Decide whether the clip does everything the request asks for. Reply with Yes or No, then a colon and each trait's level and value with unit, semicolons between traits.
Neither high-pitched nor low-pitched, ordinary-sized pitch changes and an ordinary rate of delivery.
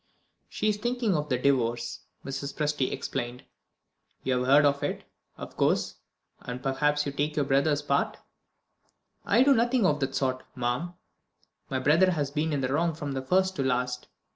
Yes: medium, 145 Hz; average, 3.4 semitones; average, 170 wpm